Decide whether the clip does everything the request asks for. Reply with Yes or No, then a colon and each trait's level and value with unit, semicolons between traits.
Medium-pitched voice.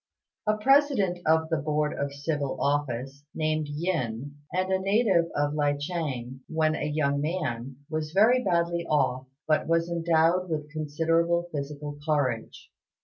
Yes: medium, 155 Hz